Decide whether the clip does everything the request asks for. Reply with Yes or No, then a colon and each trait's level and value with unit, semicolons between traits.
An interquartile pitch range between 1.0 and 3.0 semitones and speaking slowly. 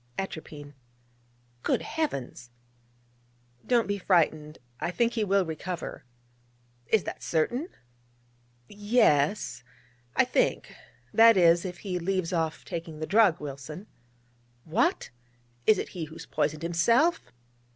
No: average, 5.1 semitones; slow, 120 wpm